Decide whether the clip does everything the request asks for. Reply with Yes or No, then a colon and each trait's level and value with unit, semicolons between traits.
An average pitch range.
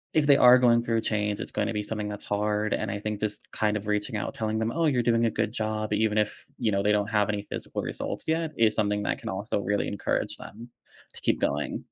No: narrow, 1.7 semitones